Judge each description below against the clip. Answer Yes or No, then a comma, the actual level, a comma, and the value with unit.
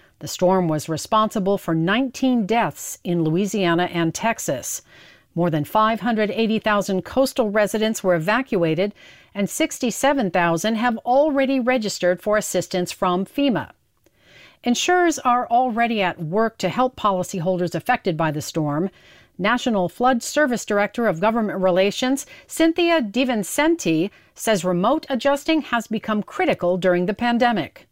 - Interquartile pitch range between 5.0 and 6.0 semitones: Yes, average, 5.3 semitones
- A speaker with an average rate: No, slow, 120 wpm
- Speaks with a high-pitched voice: Yes, high, 215 Hz